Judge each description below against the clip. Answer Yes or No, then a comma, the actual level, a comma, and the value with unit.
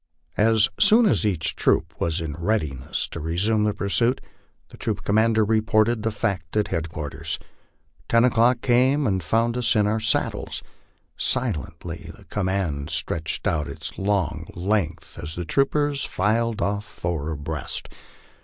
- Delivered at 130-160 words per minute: Yes, average, 145 wpm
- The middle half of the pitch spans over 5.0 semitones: Yes, wide, 5.4 semitones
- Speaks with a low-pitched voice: Yes, low, 105 Hz